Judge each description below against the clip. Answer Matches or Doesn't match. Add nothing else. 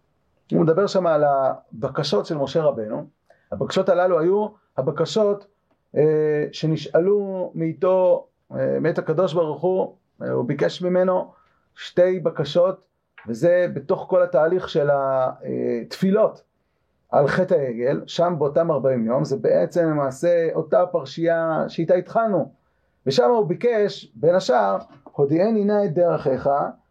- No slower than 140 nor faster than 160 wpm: Doesn't match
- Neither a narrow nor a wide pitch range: Matches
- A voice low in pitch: Doesn't match